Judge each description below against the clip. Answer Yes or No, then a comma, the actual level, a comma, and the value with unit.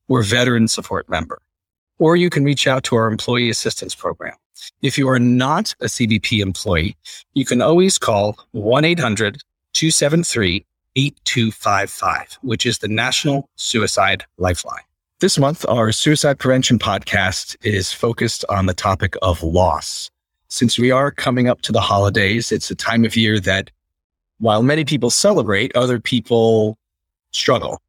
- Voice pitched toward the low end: Yes, low, 115 Hz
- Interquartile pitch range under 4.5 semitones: No, average, 4.8 semitones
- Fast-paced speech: No, average, 140 wpm